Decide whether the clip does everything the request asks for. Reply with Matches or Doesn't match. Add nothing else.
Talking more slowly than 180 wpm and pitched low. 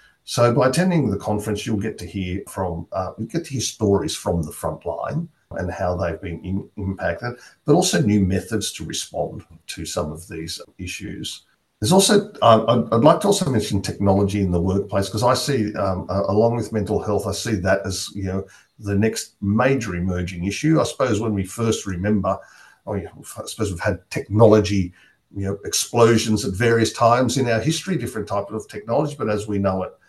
Doesn't match